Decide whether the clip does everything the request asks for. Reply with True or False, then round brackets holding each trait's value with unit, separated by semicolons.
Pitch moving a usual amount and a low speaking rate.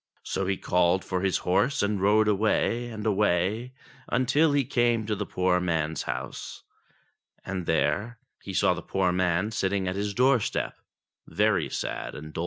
False (3.8 semitones; 165 wpm)